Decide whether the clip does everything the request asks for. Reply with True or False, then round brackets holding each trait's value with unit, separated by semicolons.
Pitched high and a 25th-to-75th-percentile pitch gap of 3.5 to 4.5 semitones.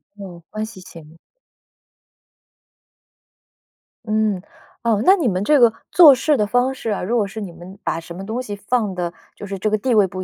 True (210 Hz; 3.9 semitones)